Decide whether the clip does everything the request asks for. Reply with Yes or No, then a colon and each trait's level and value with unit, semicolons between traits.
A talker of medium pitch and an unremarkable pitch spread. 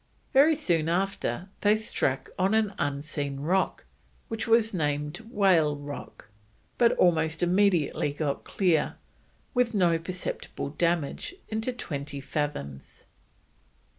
No: medium, 170 Hz; wide, 5.8 semitones